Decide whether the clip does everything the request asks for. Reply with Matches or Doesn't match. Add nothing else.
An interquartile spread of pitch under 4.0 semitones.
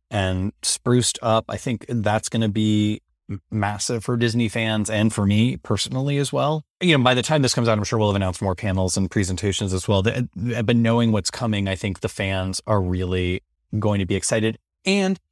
Matches